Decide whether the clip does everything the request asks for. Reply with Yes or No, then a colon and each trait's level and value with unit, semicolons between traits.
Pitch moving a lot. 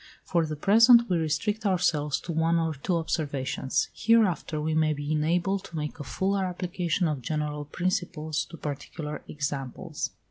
No: average, 3.3 semitones